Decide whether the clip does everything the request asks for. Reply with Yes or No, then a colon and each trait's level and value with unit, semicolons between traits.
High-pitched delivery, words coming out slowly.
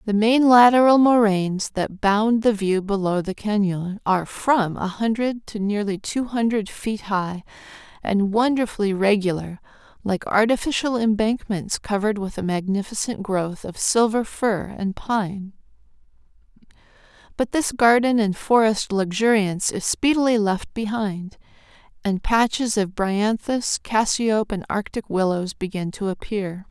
Yes: high, 210 Hz; slow, 130 wpm